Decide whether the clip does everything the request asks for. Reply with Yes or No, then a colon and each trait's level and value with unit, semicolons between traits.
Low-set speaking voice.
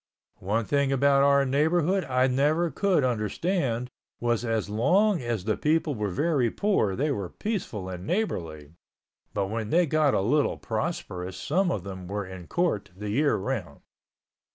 Yes: low, 125 Hz